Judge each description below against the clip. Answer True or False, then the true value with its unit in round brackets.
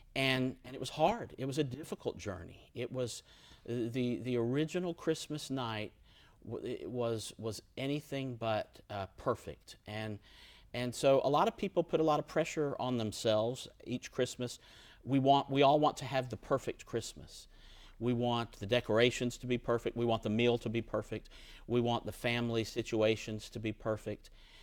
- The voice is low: True (120 Hz)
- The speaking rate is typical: True (175 wpm)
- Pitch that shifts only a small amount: False (3.4 semitones)